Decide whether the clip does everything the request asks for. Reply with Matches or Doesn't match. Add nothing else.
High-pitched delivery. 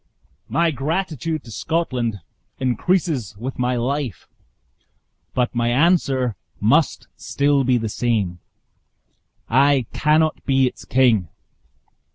Doesn't match